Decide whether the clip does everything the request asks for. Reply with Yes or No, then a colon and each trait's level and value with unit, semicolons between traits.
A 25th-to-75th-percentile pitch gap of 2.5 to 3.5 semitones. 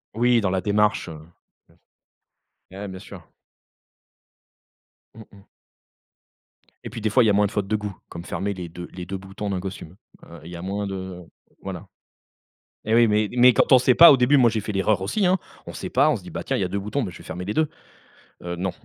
Yes: average, 3.0 semitones